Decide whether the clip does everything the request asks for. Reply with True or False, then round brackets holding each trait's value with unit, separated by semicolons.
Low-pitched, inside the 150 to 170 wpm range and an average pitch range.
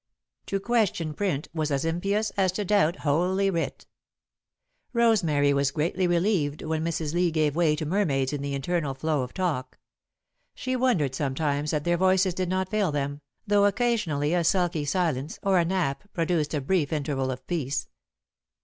False (165 Hz; 165 wpm; 4.5 semitones)